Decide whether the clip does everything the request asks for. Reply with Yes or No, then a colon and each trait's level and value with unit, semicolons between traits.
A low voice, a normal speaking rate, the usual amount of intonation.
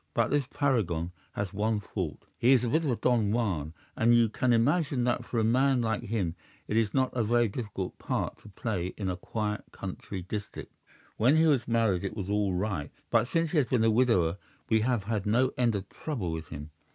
No: low, 110 Hz; fast, 220 wpm; average, 4.0 semitones